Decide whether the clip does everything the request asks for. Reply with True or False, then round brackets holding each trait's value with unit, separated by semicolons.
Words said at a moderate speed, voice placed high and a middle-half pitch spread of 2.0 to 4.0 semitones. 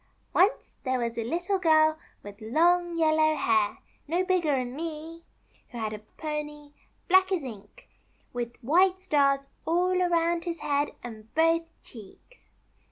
False (150 wpm; 310 Hz; 5.6 semitones)